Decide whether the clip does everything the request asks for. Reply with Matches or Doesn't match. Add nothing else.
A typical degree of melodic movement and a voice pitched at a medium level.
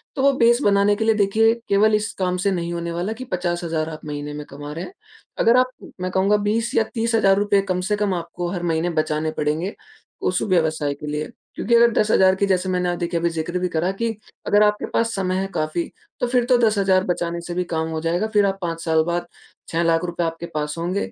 Matches